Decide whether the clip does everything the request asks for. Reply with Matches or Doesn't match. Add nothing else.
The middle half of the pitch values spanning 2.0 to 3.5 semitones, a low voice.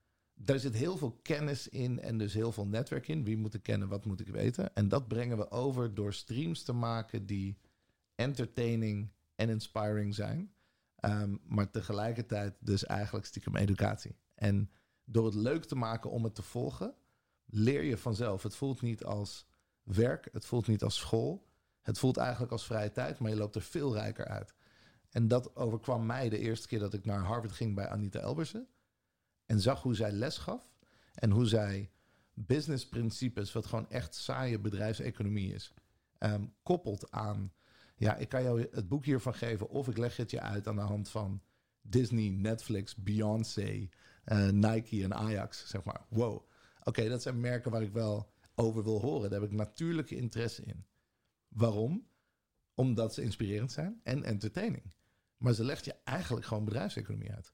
Matches